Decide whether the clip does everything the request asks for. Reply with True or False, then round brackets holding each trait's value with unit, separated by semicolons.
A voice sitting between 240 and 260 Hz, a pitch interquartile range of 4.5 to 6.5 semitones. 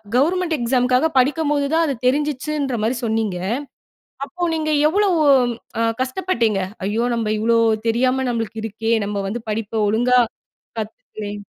True (250 Hz; 5.0 semitones)